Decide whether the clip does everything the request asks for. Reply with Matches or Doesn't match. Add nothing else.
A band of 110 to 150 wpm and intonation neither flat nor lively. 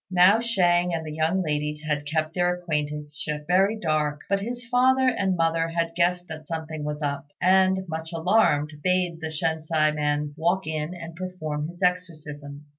Doesn't match